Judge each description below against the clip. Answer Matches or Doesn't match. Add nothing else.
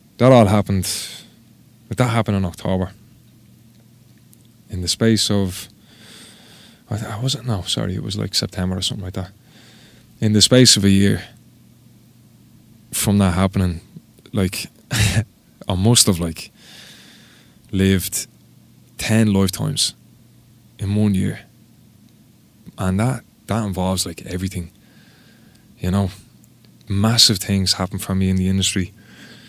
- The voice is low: Matches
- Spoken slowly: Matches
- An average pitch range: Matches